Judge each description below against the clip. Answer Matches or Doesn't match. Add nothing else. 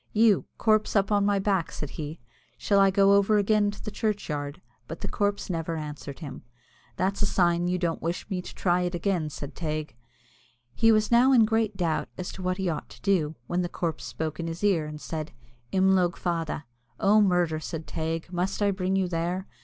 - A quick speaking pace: Matches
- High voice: Doesn't match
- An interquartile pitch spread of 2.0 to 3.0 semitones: Doesn't match